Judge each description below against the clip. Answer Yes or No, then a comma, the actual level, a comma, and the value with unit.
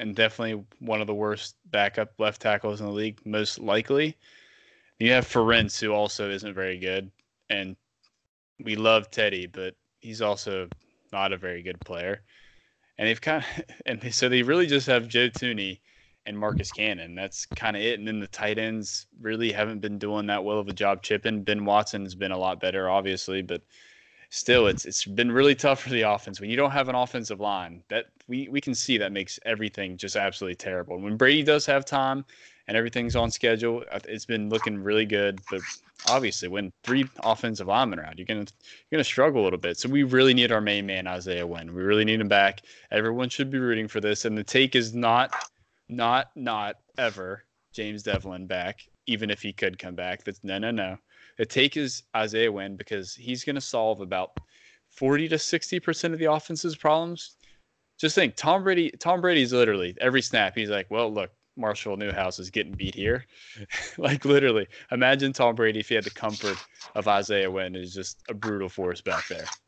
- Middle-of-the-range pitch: No, low, 110 Hz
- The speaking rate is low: No, average, 200 wpm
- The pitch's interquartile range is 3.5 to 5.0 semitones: Yes, average, 4.1 semitones